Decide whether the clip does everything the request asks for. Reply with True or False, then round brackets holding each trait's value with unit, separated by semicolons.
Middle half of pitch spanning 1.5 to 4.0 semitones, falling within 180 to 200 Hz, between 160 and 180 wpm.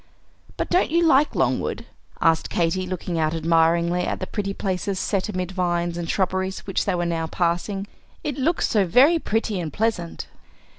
True (3.4 semitones; 185 Hz; 170 wpm)